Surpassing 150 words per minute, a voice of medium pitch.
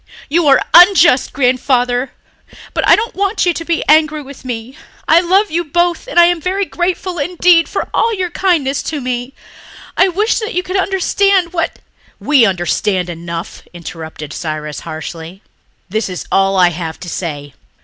No: average, 170 wpm; very high, 285 Hz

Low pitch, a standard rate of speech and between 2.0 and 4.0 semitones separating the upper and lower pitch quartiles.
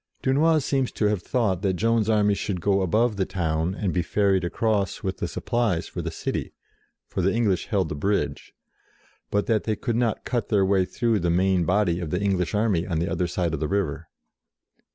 No: low, 100 Hz; fast, 210 wpm; average, 3.6 semitones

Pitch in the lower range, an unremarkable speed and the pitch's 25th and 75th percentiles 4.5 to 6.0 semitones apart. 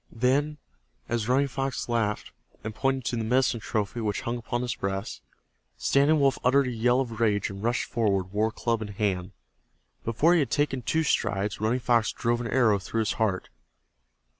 No: low, 115 Hz; average, 185 wpm; average, 3.5 semitones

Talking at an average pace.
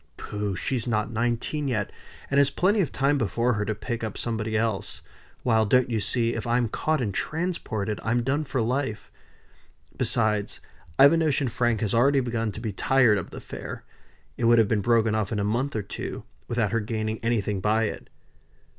Yes: average, 195 wpm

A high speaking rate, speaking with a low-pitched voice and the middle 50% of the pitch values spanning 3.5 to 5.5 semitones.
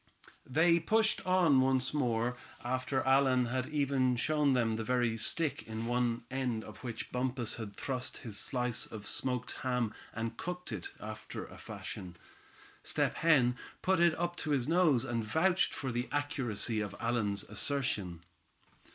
No: average, 155 wpm; low, 125 Hz; average, 3.8 semitones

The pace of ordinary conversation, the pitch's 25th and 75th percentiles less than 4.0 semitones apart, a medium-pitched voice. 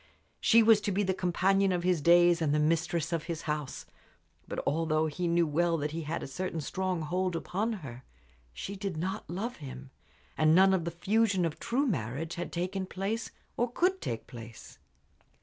Yes: average, 190 wpm; average, 3.6 semitones; medium, 175 Hz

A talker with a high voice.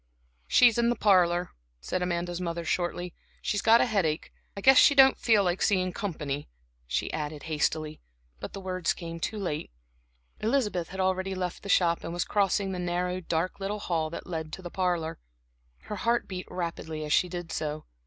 No: medium, 180 Hz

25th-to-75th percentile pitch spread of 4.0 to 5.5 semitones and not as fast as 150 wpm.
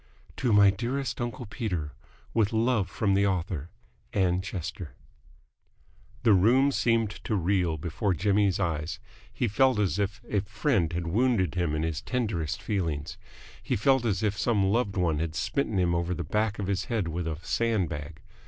No: average, 4.5 semitones; average, 170 wpm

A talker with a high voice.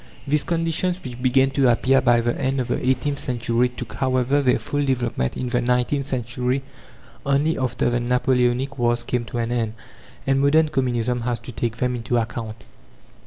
No: low, 125 Hz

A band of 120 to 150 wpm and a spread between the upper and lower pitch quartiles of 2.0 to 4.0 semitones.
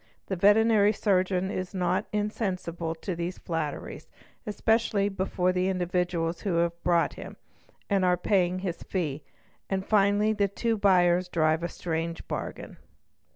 Yes: average, 140 wpm; average, 2.7 semitones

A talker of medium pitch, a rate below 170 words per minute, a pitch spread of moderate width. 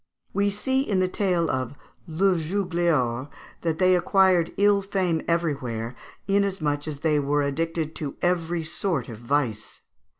Yes: medium, 165 Hz; average, 140 wpm; average, 4.5 semitones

